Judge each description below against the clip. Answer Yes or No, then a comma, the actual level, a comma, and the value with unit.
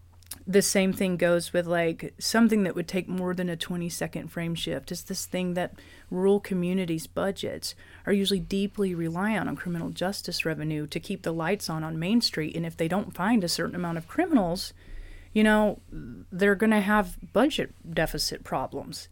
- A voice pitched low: No, medium, 180 Hz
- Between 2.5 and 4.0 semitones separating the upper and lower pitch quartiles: Yes, average, 3.1 semitones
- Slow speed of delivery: No, average, 185 wpm